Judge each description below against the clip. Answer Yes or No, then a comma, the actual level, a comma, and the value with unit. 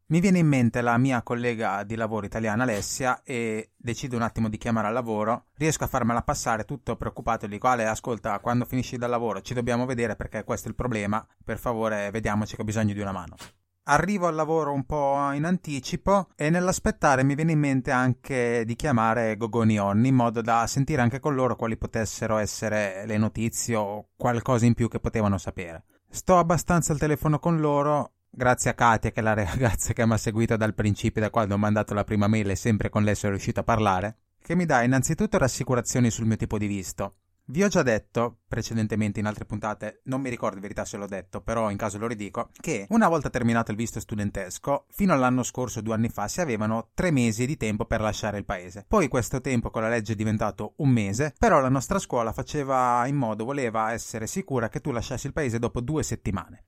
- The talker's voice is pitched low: Yes, low, 115 Hz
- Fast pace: Yes, fast, 215 wpm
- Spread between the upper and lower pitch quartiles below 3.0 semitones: No, average, 3.4 semitones